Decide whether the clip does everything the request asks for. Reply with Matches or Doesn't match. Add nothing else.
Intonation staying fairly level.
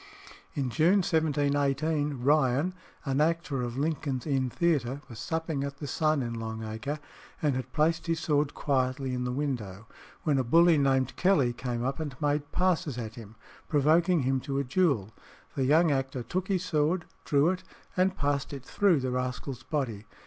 Doesn't match